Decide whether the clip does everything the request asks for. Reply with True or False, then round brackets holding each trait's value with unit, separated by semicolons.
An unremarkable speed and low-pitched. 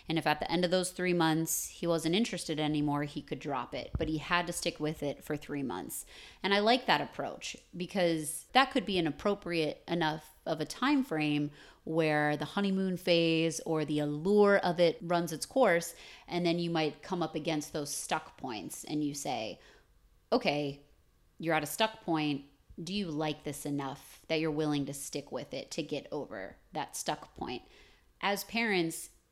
False (190 wpm; 160 Hz)